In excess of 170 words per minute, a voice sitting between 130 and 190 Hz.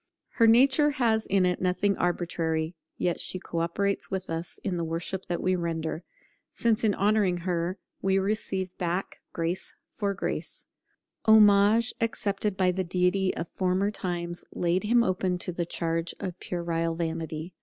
No: average, 155 wpm; medium, 185 Hz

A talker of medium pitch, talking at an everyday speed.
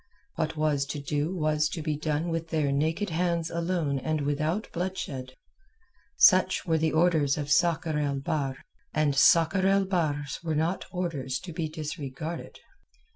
Yes: medium, 155 Hz; average, 155 wpm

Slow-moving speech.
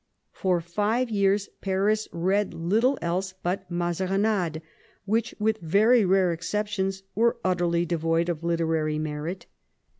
Yes: slow, 120 wpm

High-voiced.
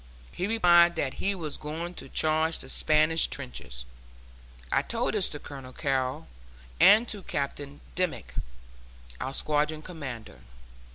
No: medium, 155 Hz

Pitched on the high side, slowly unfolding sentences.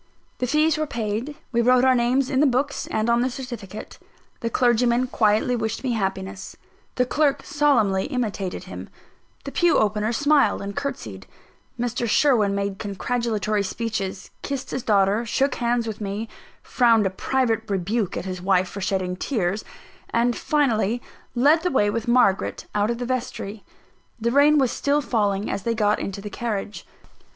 No: high, 230 Hz; average, 165 wpm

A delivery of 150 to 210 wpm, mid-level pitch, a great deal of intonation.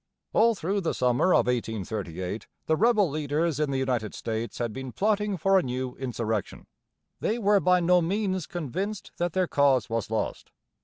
Yes: average, 170 wpm; medium, 150 Hz; wide, 7.9 semitones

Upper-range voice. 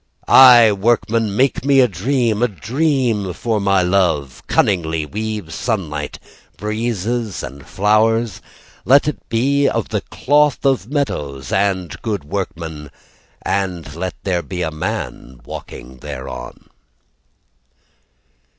No: low, 100 Hz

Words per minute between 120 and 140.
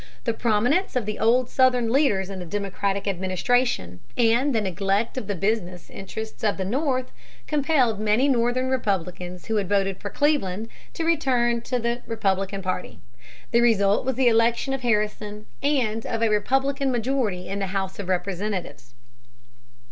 No: average, 160 wpm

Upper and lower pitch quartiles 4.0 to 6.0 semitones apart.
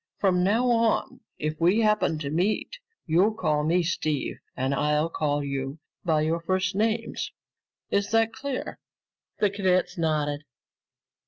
Yes: wide, 5.6 semitones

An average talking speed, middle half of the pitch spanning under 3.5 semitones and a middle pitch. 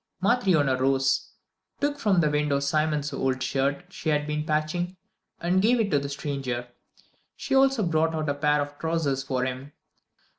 No: average, 170 wpm; average, 3.9 semitones; medium, 150 Hz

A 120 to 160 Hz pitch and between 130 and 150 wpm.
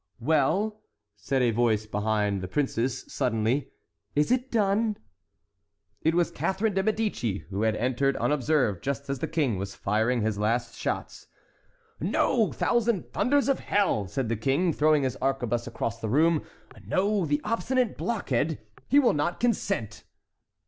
Yes: medium, 140 Hz; average, 145 wpm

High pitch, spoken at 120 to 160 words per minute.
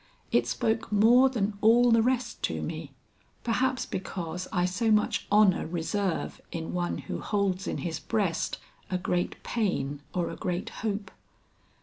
Yes: high, 200 Hz; average, 150 wpm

